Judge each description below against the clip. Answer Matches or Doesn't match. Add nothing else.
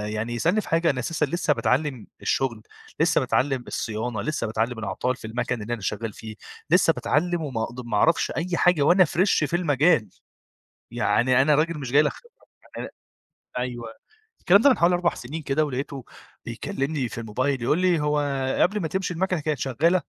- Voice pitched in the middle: Matches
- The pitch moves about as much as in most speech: Doesn't match